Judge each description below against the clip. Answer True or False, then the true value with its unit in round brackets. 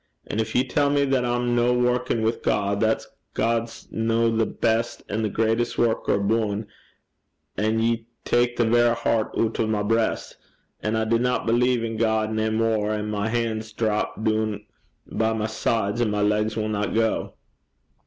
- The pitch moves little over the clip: True (1.4 semitones)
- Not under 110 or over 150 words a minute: False (175 wpm)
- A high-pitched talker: False (110 Hz)